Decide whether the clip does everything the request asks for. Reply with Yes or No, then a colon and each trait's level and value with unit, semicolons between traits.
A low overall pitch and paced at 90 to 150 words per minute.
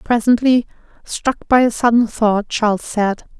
No: high, 225 Hz; average, 140 wpm